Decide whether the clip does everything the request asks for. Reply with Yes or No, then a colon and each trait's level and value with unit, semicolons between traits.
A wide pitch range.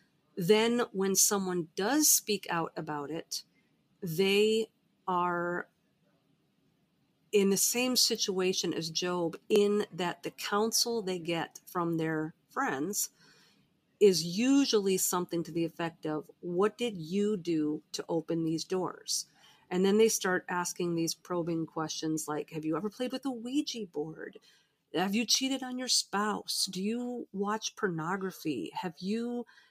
No: average, 4.4 semitones